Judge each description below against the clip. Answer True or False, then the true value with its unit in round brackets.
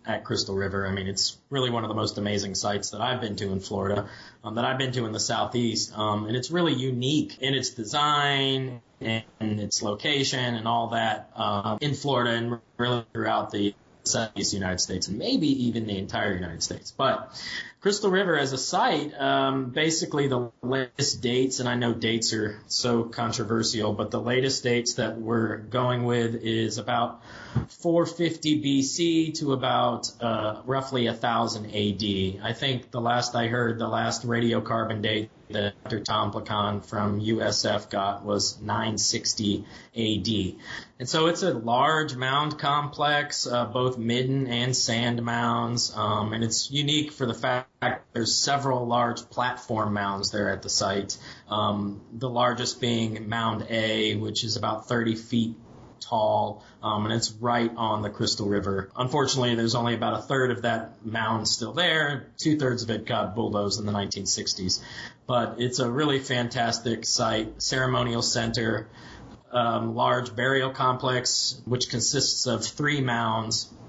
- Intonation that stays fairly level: False (3.0 semitones)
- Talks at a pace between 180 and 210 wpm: False (160 wpm)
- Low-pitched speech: True (115 Hz)